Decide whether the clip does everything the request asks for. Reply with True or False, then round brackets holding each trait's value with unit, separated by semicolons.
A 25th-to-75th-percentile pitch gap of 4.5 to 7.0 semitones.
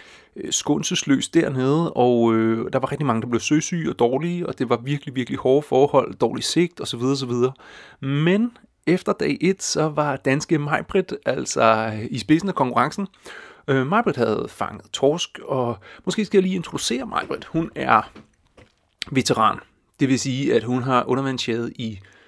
True (5.2 semitones)